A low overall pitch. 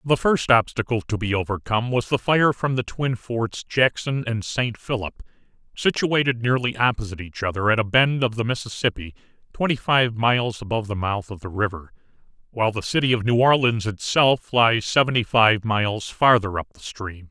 Yes: low, 115 Hz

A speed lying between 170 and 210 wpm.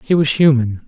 Yes: fast, 205 wpm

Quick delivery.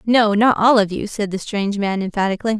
Yes: fast, 230 wpm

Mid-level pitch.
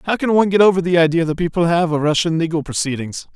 Yes: medium, 165 Hz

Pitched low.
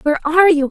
No: very high, 320 Hz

